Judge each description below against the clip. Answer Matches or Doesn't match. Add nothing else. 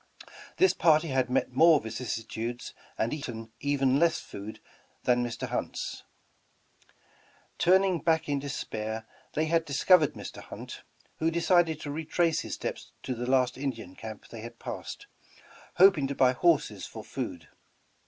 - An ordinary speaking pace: Matches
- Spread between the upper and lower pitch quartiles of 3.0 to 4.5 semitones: Doesn't match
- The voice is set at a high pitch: Doesn't match